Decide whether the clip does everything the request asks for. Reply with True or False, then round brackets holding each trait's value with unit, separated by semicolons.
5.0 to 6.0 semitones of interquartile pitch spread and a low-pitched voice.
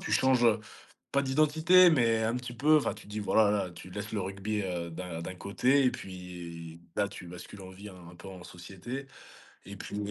True (5.3 semitones; 100 Hz)